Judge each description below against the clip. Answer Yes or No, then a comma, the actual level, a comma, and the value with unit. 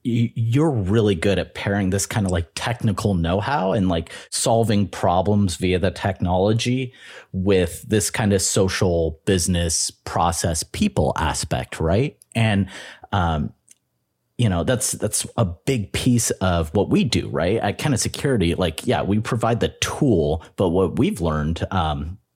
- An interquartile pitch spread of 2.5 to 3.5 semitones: No, average, 4.2 semitones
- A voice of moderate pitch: No, very low, 95 Hz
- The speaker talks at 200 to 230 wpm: No, average, 155 wpm